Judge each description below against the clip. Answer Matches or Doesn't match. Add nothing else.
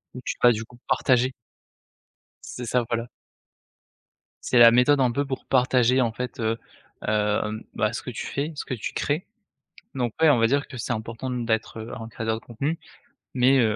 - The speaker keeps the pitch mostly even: Matches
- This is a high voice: Doesn't match